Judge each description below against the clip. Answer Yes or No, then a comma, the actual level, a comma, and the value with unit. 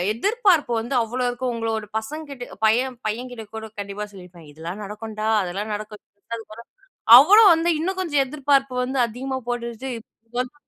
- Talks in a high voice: Yes, high, 245 Hz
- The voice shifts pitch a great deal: No, average, 4.3 semitones